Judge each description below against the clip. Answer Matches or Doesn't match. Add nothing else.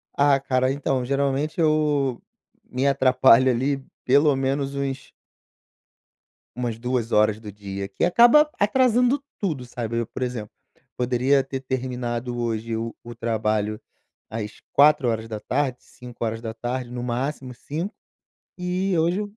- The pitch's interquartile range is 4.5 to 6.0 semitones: Doesn't match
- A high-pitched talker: Doesn't match